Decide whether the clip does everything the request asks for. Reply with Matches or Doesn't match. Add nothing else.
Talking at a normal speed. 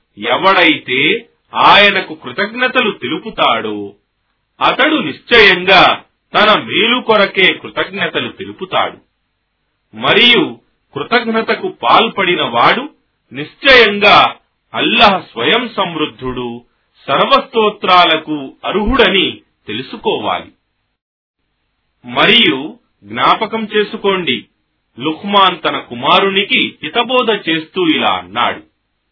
Doesn't match